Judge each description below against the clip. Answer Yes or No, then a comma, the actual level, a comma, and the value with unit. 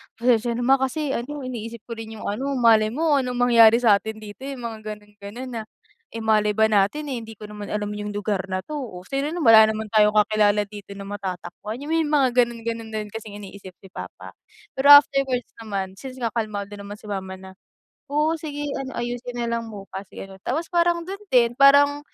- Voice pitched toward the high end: Yes, high, 225 Hz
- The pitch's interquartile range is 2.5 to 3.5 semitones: No, average, 4.2 semitones